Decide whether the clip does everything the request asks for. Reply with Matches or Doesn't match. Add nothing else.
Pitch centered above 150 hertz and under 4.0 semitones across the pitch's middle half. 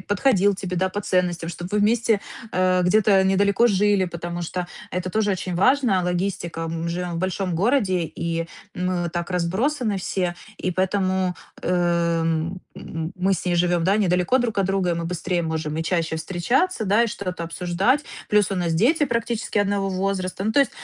Matches